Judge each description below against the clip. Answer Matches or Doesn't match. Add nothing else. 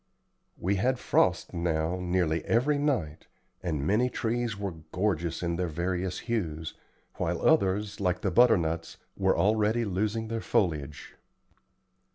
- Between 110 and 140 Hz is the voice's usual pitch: Doesn't match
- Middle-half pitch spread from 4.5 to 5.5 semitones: Matches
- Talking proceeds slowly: Matches